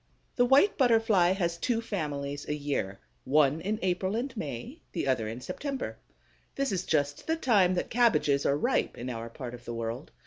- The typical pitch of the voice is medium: Yes, medium, 170 Hz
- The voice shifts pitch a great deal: Yes, wide, 8.6 semitones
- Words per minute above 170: Yes, average, 185 wpm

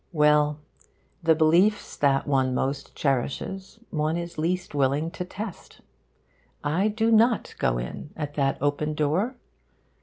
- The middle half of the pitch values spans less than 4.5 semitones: Yes, average, 4.1 semitones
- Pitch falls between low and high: Yes, medium, 155 Hz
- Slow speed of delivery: Yes, slow, 130 wpm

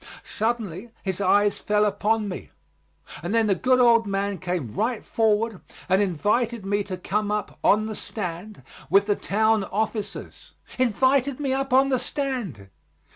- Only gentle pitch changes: No, average, 3.1 semitones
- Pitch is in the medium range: No, high, 210 Hz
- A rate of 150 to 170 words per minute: Yes, average, 155 wpm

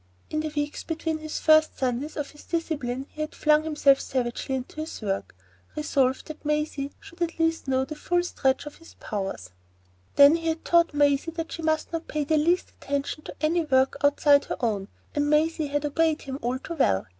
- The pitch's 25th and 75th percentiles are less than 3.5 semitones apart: Yes, average, 2.8 semitones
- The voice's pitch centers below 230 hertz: No, very high, 300 Hz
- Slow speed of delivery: No, fast, 205 wpm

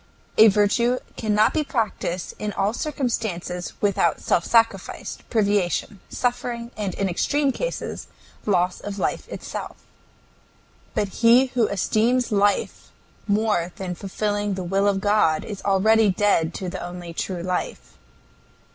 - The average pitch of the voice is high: Yes, high, 205 Hz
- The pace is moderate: No, slow, 130 wpm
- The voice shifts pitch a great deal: No, average, 3.4 semitones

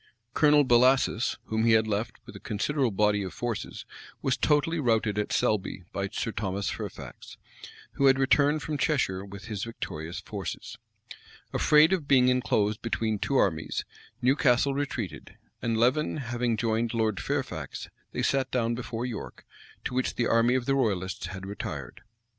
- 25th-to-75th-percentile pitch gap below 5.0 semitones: Yes, average, 4.2 semitones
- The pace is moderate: Yes, average, 160 wpm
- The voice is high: No, low, 115 Hz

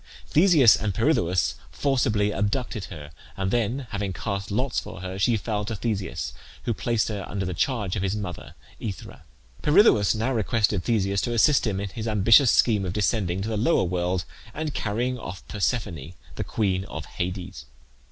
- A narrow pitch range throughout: No, average, 3.8 semitones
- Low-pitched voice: Yes, low, 105 Hz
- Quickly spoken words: No, average, 170 wpm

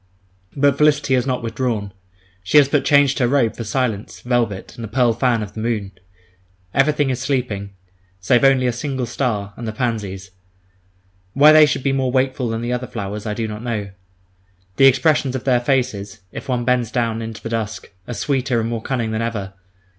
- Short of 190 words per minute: No, average, 195 wpm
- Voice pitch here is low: Yes, low, 120 Hz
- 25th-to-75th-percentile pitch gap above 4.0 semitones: No, average, 3.2 semitones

